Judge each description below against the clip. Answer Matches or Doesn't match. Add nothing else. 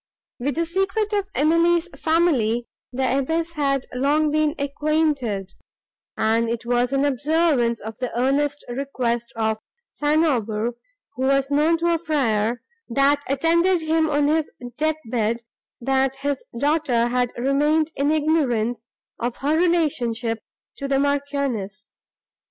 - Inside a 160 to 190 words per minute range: Doesn't match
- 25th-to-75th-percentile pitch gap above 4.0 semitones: Matches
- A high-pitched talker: Matches